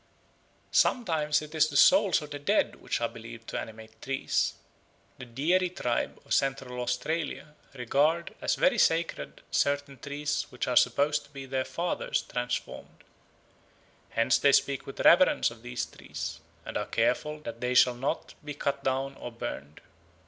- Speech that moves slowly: No, average, 160 wpm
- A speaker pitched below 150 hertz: Yes, medium, 140 Hz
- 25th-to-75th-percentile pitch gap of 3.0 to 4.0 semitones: Yes, average, 3.7 semitones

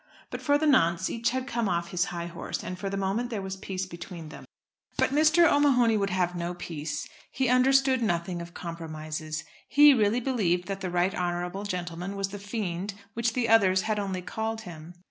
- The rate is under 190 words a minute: No, average, 200 wpm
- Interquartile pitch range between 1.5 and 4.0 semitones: No, average, 4.8 semitones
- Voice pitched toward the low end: No, high, 195 Hz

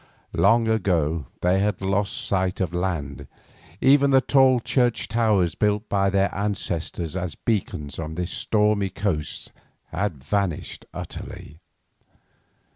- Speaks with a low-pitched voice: Yes, very low, 95 Hz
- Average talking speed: No, slow, 120 wpm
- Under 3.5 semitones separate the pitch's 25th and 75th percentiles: No, average, 3.8 semitones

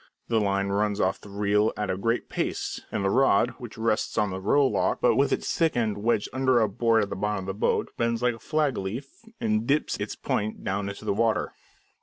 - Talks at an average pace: No, fast, 235 wpm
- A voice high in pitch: No, low, 110 Hz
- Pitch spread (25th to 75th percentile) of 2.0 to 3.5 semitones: Yes, average, 2.8 semitones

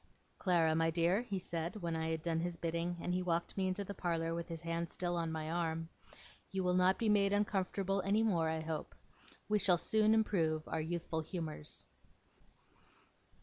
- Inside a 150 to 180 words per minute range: No, average, 190 wpm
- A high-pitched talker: No, medium, 170 Hz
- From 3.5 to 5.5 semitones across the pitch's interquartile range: No, average, 2.8 semitones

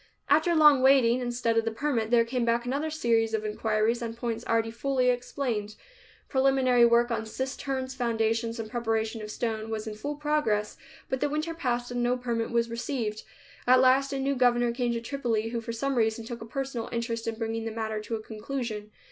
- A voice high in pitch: Yes, high, 235 Hz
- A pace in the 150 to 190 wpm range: No, average, 200 wpm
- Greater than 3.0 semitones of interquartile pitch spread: No, narrow, 2.5 semitones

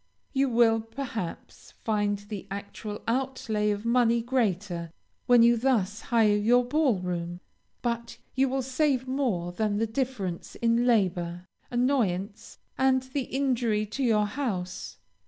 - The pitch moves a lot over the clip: No, average, 3.7 semitones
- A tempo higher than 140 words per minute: No, slow, 135 wpm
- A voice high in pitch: Yes, high, 225 Hz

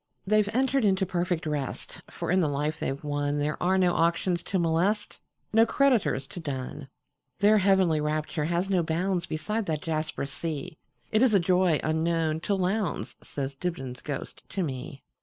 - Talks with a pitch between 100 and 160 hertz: No, medium, 170 Hz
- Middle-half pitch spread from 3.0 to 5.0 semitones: Yes, average, 4.2 semitones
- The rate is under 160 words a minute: Yes, average, 150 wpm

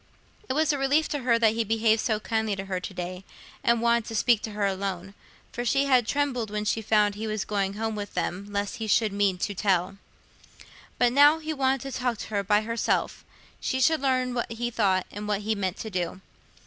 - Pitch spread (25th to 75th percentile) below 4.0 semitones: Yes, average, 3.5 semitones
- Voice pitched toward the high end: Yes, high, 220 Hz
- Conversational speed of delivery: No, fast, 225 wpm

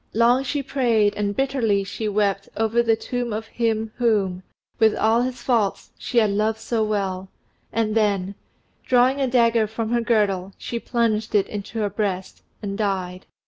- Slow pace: No, average, 170 wpm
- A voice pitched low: No, high, 220 Hz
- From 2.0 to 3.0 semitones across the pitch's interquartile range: Yes, average, 2.7 semitones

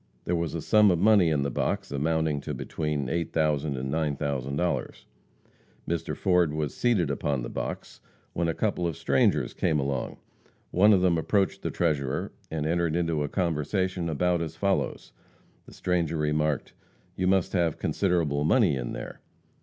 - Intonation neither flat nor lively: Yes, average, 3.3 semitones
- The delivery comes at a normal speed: Yes, average, 160 wpm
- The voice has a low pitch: Yes, very low, 80 Hz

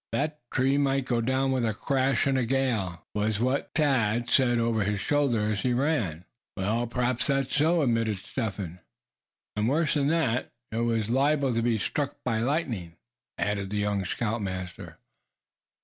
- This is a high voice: No, low, 120 Hz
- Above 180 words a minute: No, average, 165 wpm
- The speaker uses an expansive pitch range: No, average, 4.4 semitones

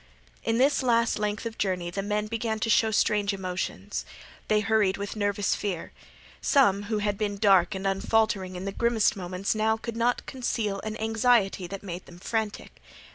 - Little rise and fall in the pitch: Yes, narrow, 2.3 semitones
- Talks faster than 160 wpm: Yes, average, 180 wpm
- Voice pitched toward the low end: No, high, 210 Hz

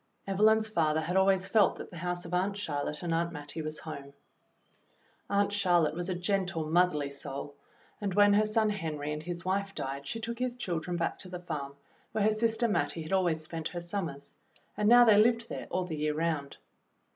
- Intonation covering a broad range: No, average, 4.5 semitones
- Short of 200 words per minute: No, fast, 205 wpm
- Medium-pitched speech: Yes, medium, 175 Hz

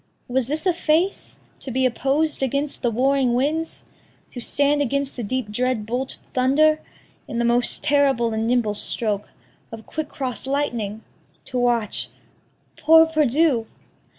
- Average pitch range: Yes, average, 3.5 semitones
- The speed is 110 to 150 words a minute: Yes, average, 145 wpm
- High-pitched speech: Yes, very high, 260 Hz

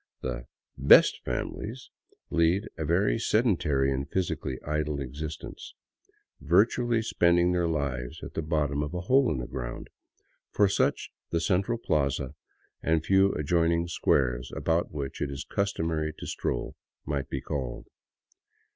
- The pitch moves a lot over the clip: No, average, 4.6 semitones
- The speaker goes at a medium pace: Yes, average, 145 wpm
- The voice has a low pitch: Yes, very low, 80 Hz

